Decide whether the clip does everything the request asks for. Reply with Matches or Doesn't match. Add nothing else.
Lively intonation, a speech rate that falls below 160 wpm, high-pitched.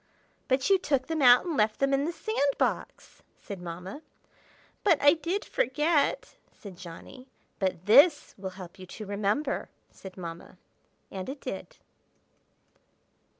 Matches